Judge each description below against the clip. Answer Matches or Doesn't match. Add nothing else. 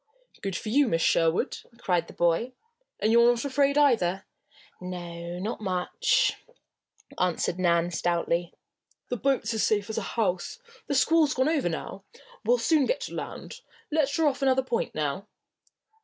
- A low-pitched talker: Doesn't match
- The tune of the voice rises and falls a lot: Matches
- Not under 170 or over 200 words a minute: Doesn't match